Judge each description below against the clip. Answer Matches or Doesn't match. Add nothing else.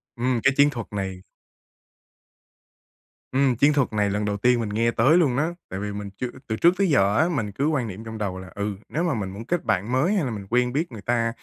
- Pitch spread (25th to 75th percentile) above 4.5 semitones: Matches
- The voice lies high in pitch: Doesn't match